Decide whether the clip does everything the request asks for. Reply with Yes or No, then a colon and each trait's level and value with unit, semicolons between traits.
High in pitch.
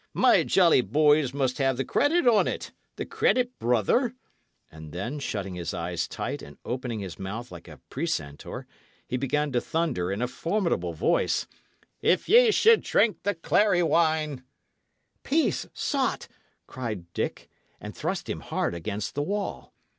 No: low, 135 Hz